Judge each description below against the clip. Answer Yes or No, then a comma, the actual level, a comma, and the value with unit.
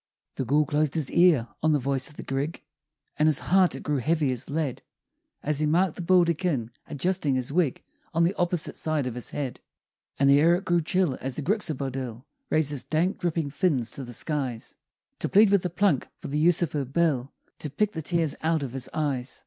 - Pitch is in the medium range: Yes, medium, 150 Hz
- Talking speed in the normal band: No, fast, 215 wpm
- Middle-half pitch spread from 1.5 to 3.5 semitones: No, average, 4.1 semitones